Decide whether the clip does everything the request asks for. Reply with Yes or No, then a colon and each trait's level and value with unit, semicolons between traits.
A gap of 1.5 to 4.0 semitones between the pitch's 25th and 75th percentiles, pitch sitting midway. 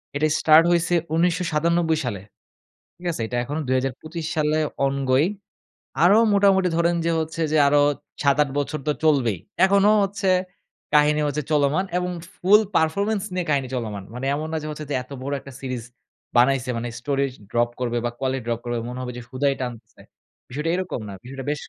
No: average, 4.5 semitones; medium, 150 Hz